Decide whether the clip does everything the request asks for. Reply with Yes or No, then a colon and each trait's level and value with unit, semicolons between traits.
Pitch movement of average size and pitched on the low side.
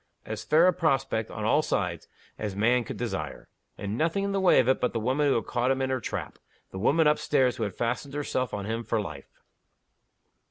Yes: average, 5.0 semitones; low, 125 Hz